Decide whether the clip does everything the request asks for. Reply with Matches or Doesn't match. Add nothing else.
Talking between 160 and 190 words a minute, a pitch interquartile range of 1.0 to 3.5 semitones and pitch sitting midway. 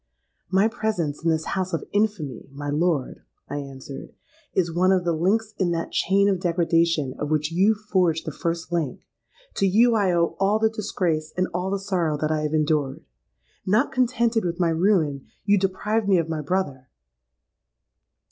Doesn't match